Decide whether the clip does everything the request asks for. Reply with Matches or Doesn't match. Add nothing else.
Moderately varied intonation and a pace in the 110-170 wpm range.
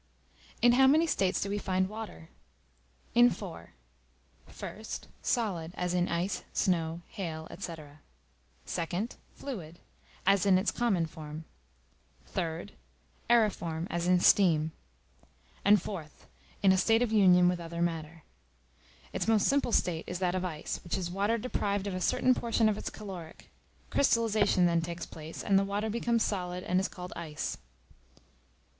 Matches